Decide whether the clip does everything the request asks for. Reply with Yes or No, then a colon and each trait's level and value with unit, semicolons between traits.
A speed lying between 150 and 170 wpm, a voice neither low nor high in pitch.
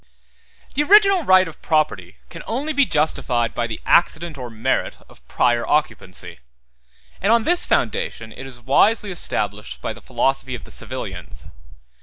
Yes: average, 155 wpm; medium, 155 Hz